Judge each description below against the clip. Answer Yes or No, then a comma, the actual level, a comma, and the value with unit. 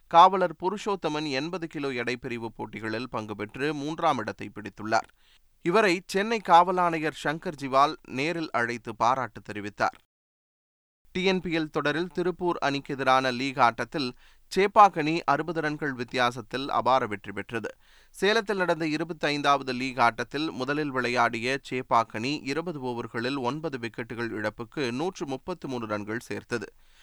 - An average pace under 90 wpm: No, average, 115 wpm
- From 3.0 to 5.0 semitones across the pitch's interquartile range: No, wide, 5.6 semitones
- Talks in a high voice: No, low, 135 Hz